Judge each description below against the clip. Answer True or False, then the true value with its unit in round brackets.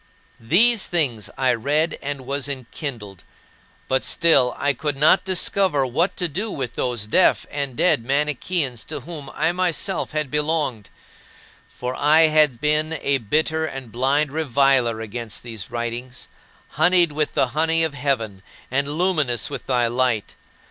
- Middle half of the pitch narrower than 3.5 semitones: False (4.3 semitones)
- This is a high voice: False (140 Hz)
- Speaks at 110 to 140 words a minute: False (150 wpm)